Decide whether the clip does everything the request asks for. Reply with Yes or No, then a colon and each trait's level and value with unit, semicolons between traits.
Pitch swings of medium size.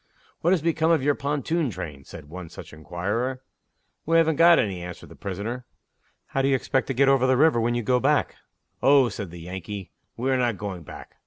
No: wide, 6.8 semitones